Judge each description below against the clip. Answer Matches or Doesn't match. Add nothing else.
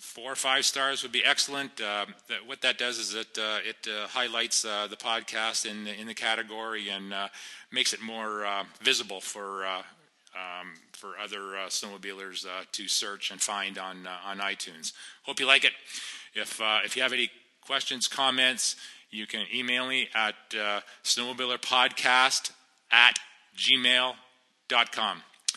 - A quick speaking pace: Doesn't match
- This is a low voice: Matches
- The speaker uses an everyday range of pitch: Matches